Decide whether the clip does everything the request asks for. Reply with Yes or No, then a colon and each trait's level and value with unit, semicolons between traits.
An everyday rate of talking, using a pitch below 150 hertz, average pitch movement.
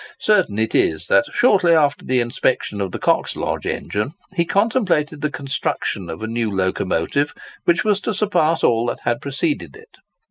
No: average, 170 wpm; medium, 140 Hz; wide, 7.7 semitones